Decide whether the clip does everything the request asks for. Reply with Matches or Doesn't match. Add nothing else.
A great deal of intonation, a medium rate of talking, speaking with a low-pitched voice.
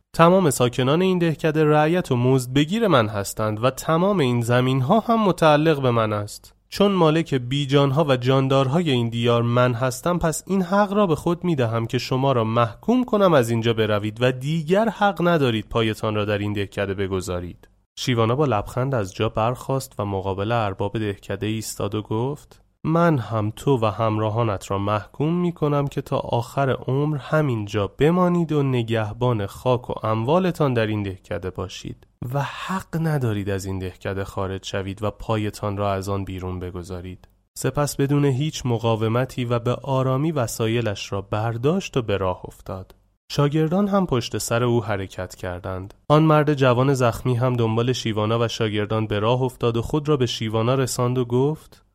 Doesn't match